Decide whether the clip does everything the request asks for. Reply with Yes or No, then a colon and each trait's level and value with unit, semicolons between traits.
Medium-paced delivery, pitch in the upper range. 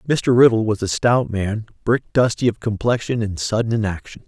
No: average, 195 wpm; low, 110 Hz